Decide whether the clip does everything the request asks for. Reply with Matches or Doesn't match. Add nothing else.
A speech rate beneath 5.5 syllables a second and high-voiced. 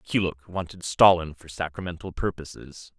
Doesn't match